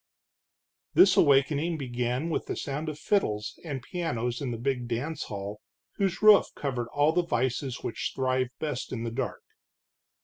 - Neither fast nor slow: Yes, average, 160 wpm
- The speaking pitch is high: No, low, 135 Hz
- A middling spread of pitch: Yes, average, 4.5 semitones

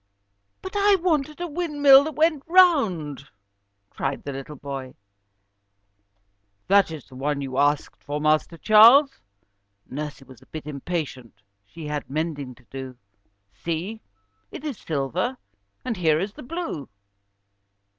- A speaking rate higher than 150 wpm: No, slow, 135 wpm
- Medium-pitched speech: Yes, medium, 160 Hz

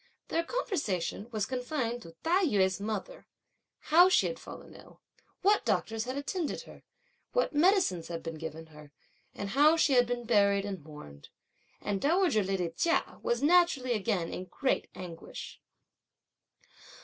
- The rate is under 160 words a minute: Yes, average, 150 wpm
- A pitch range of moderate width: No, wide, 9.0 semitones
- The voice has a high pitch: Yes, high, 230 Hz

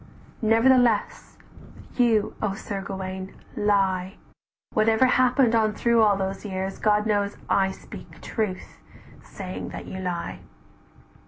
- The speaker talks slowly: Yes, slow, 115 wpm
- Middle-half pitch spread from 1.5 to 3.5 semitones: Yes, average, 2.7 semitones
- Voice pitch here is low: No, high, 205 Hz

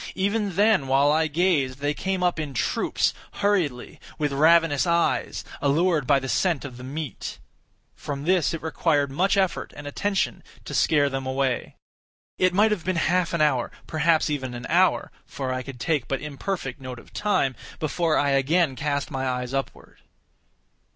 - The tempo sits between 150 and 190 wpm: Yes, average, 170 wpm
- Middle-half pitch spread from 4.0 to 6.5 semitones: Yes, average, 4.4 semitones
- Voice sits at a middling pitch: Yes, medium, 150 Hz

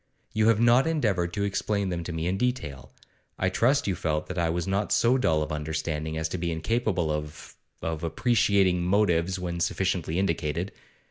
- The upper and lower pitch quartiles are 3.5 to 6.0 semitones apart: Yes, average, 4.0 semitones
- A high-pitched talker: No, very low, 90 Hz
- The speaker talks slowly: No, average, 185 wpm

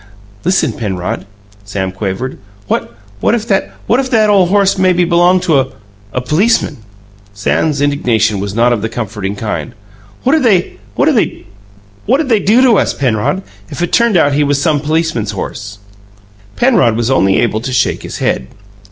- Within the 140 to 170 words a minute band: Yes, average, 155 wpm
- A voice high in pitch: No, low, 135 Hz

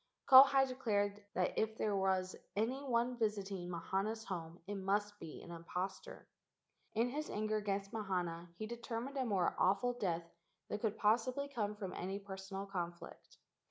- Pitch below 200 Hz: No, high, 205 Hz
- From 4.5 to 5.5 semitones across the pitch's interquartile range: No, average, 3.3 semitones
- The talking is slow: No, average, 160 wpm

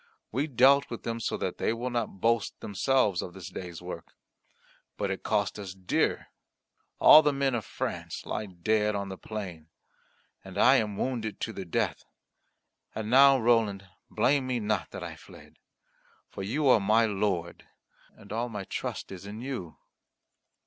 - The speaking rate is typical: Yes, average, 170 wpm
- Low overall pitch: Yes, low, 110 Hz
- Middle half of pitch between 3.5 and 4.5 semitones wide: Yes, average, 4.0 semitones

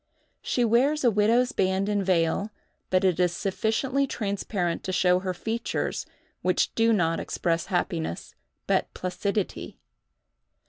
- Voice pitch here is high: Yes, high, 195 Hz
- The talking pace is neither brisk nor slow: No, slow, 130 wpm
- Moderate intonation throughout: Yes, average, 4.0 semitones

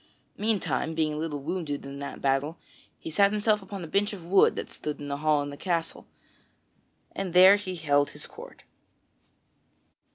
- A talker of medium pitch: Yes, medium, 165 Hz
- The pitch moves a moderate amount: Yes, average, 5.0 semitones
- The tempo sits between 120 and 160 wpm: No, average, 185 wpm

